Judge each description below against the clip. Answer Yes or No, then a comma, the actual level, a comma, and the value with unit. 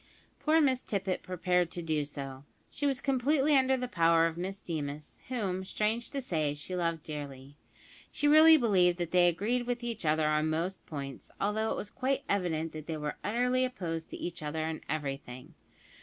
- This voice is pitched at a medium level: Yes, medium, 180 Hz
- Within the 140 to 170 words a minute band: No, average, 185 wpm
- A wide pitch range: Yes, wide, 7.5 semitones